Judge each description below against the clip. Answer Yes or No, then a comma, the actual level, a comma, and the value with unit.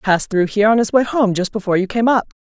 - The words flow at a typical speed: No, fast, 320 wpm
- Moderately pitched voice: No, high, 210 Hz